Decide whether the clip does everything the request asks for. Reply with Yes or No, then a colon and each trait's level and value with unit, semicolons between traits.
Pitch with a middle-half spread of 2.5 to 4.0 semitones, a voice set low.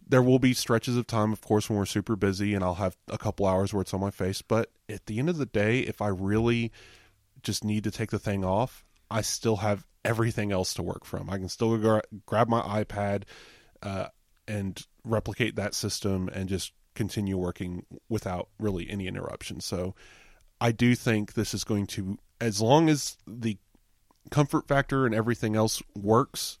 Yes: average, 2.8 semitones; low, 105 Hz